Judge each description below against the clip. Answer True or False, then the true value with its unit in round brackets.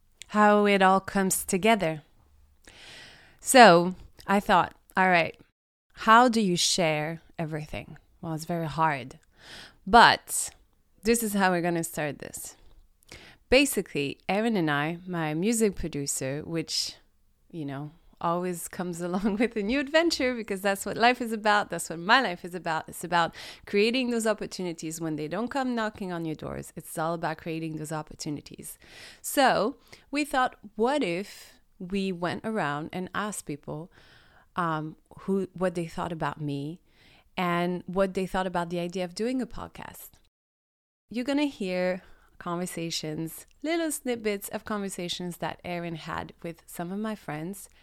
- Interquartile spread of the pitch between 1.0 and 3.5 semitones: False (4.7 semitones)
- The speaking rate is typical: True (155 wpm)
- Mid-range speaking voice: True (180 Hz)